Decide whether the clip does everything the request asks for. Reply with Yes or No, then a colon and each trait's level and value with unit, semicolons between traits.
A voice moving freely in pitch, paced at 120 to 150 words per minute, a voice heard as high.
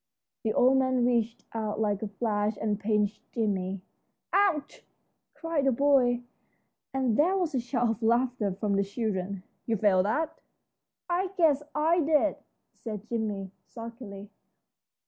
No: average, 4.5 semitones; average, 140 wpm; high, 230 Hz